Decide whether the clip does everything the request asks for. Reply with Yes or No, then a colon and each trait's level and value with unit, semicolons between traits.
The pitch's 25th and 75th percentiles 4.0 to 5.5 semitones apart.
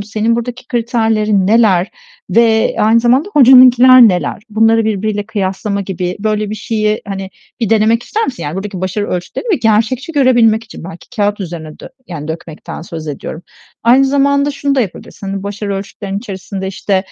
No: average, 3.5 semitones